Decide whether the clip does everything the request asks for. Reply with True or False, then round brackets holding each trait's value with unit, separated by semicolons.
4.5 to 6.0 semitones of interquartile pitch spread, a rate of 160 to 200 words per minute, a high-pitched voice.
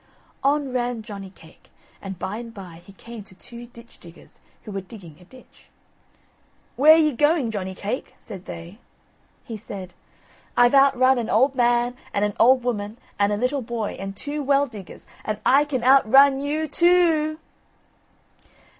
True (5.2 semitones; 170 wpm; 240 Hz)